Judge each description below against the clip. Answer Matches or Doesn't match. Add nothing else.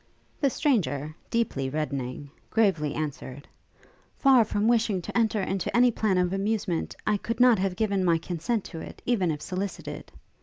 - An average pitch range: Doesn't match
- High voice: Matches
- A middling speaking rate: Matches